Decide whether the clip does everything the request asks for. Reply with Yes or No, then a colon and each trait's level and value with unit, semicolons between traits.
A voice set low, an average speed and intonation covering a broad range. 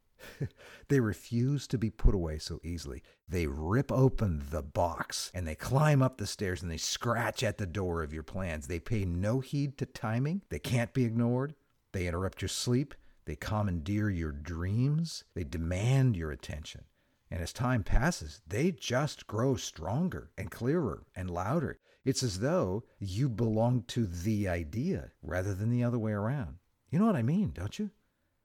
Yes: low, 105 Hz; average, 175 wpm; wide, 6.7 semitones